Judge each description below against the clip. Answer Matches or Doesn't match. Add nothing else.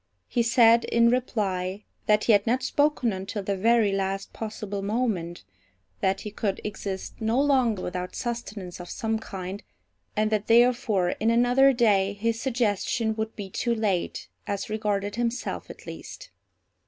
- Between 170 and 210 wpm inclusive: Doesn't match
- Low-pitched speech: Doesn't match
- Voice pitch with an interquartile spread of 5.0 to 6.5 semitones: Doesn't match